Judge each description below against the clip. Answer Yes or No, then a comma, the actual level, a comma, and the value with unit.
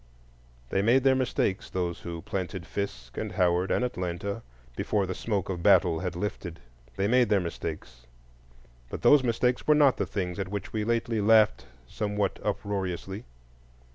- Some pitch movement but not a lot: Yes, average, 3.9 semitones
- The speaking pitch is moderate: No, low, 100 Hz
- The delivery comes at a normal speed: Yes, average, 160 wpm